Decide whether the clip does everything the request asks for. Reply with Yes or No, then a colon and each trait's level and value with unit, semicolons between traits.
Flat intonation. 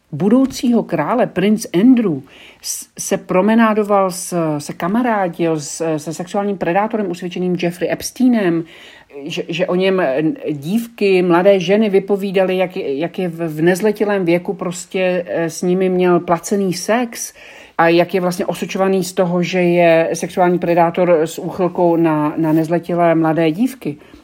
No: average, 3.0 semitones